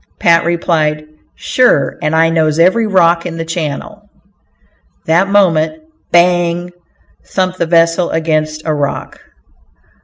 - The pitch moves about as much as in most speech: No, narrow, 2.1 semitones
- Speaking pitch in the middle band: Yes, medium, 170 Hz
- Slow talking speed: Yes, slow, 120 wpm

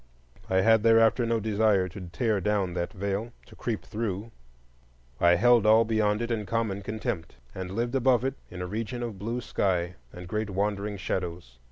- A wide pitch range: No, average, 3.3 semitones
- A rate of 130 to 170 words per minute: No, average, 180 wpm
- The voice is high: No, low, 105 Hz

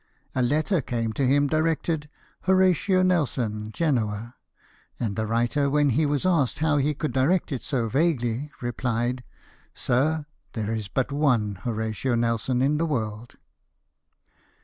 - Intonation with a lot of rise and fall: No, average, 4.6 semitones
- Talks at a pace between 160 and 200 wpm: No, average, 150 wpm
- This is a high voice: No, low, 130 Hz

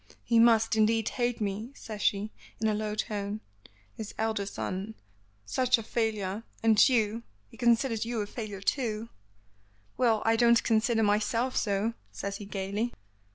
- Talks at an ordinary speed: Yes, average, 155 wpm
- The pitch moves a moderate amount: No, narrow, 1.9 semitones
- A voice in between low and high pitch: No, high, 220 Hz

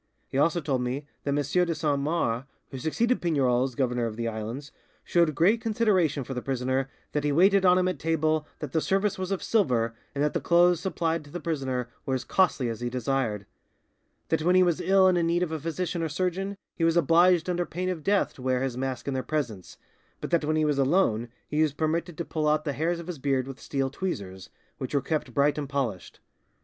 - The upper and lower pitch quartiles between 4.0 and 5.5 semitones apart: Yes, average, 4.7 semitones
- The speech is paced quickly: Yes, fast, 230 wpm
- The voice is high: No, medium, 150 Hz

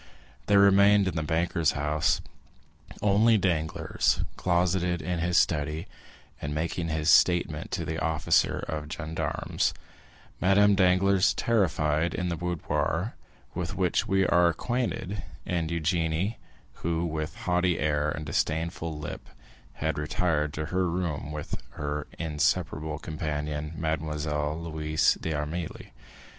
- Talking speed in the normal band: No, slow, 120 wpm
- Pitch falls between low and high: No, very low, 80 Hz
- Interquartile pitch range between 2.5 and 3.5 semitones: Yes, average, 2.9 semitones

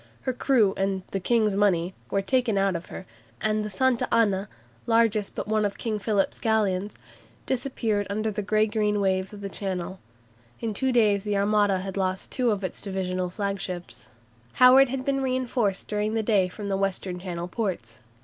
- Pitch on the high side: Yes, high, 205 Hz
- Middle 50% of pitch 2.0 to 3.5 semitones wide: Yes, narrow, 2.6 semitones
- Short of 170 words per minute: No, average, 180 wpm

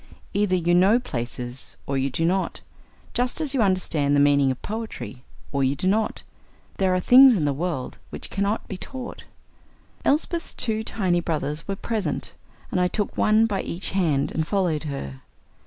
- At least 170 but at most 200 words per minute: Yes, average, 175 wpm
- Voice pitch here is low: No, medium, 180 Hz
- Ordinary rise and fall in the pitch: No, wide, 6.8 semitones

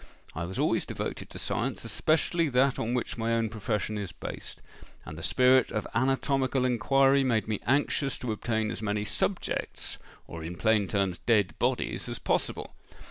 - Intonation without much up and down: No, average, 4.0 semitones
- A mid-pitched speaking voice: No, low, 115 Hz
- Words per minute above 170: No, average, 160 wpm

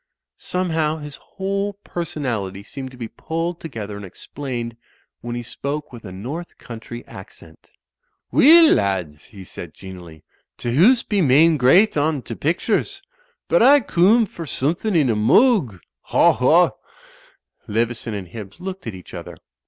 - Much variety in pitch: Yes, wide, 8.5 semitones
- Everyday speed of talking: Yes, average, 145 wpm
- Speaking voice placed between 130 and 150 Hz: Yes, low, 135 Hz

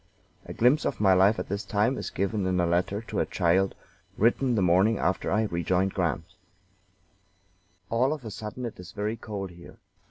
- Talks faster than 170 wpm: Yes, average, 190 wpm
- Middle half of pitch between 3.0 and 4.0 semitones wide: Yes, average, 3.4 semitones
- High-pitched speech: No, low, 100 Hz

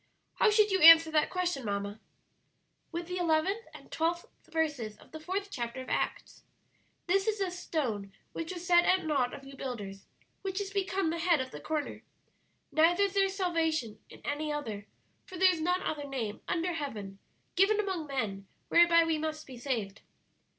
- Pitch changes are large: Yes, wide, 5.8 semitones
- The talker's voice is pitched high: Yes, very high, 320 Hz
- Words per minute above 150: Yes, average, 180 wpm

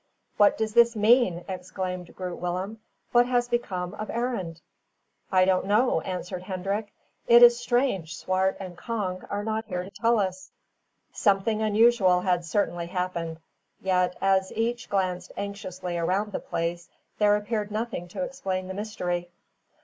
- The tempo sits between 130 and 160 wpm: Yes, average, 150 wpm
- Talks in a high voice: Yes, high, 195 Hz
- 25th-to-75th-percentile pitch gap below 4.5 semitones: Yes, average, 3.3 semitones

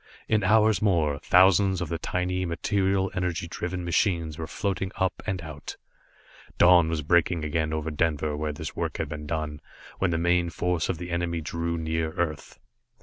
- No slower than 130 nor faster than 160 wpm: No, average, 175 wpm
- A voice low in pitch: Yes, very low, 85 Hz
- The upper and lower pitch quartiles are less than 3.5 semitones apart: Yes, narrow, 2.5 semitones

